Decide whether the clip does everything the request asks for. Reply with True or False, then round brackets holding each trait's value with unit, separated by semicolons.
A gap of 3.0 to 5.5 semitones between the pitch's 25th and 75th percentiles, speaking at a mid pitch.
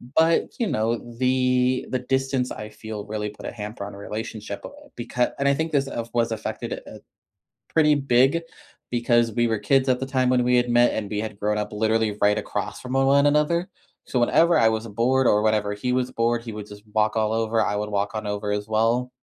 False (3.3 semitones; 115 Hz)